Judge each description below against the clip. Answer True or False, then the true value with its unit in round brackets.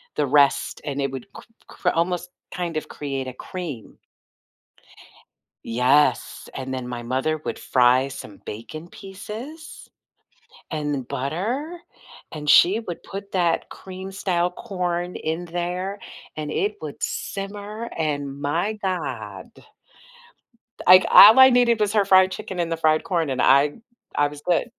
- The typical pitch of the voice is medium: True (170 Hz)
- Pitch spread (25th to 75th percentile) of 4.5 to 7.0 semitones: True (5.4 semitones)